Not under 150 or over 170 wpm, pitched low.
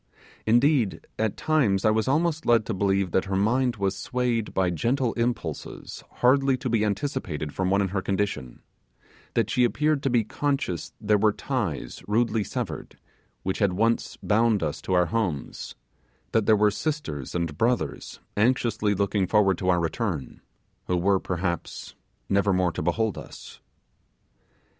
Yes: average, 155 wpm; low, 105 Hz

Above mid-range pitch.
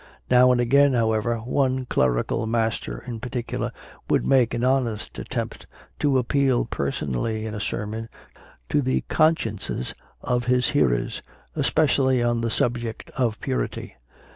No: low, 120 Hz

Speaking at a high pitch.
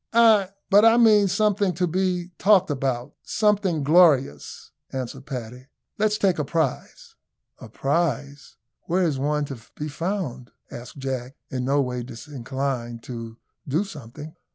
No: medium, 145 Hz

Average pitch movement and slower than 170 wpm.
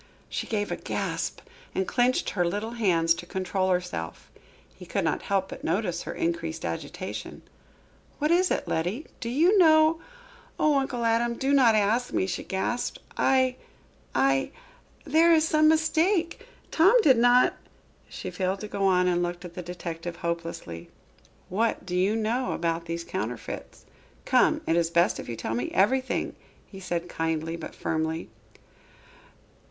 No: wide, 7.4 semitones; average, 160 wpm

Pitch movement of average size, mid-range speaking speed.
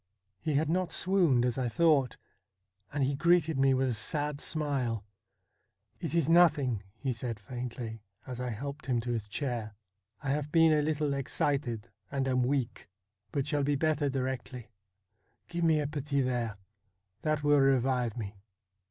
Yes: average, 3.5 semitones; average, 170 wpm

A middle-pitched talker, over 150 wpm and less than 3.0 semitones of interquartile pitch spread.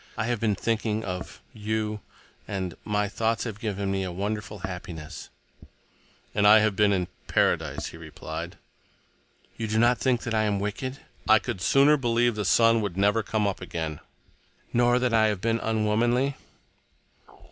No: low, 105 Hz; average, 160 wpm; narrow, 2.6 semitones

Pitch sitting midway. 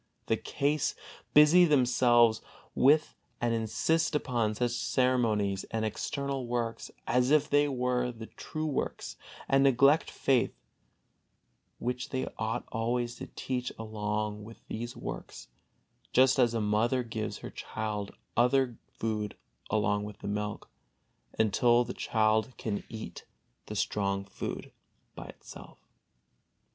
No: low, 120 Hz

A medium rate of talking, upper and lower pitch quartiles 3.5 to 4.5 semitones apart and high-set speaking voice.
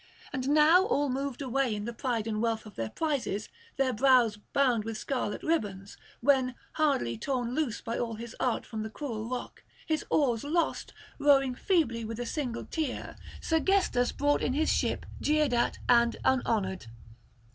Yes: average, 170 wpm; average, 4.2 semitones; very high, 250 Hz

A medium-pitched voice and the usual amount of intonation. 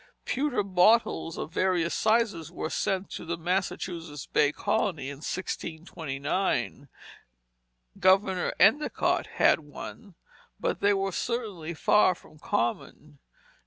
Yes: medium, 180 Hz; average, 4.0 semitones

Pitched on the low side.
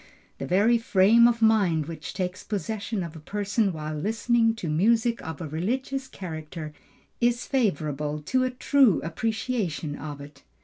No: high, 195 Hz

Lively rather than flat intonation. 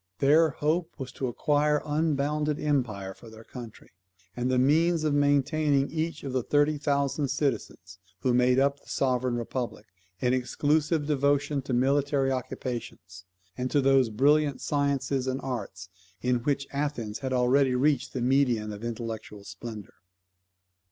No: average, 3.0 semitones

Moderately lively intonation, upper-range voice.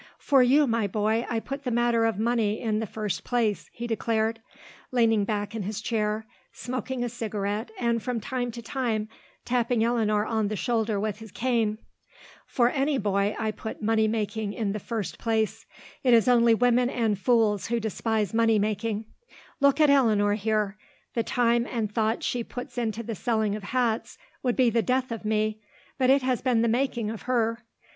No: narrow, 2.1 semitones; high, 225 Hz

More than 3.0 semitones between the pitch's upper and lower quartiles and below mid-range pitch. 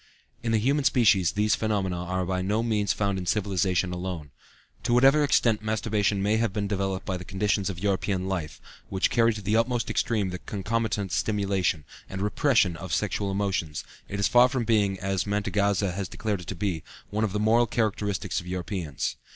No: average, 2.7 semitones; low, 100 Hz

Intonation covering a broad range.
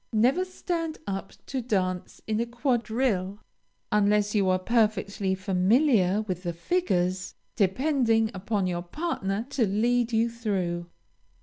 No: average, 4.2 semitones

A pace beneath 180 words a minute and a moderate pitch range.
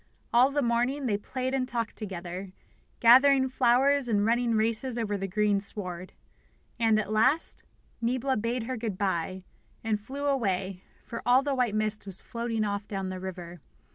Yes: average, 170 wpm; average, 4.0 semitones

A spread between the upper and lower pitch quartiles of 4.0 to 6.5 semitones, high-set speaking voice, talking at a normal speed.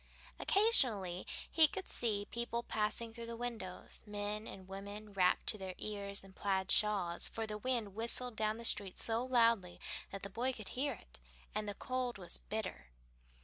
No: average, 3.1 semitones; high, 215 Hz; average, 170 wpm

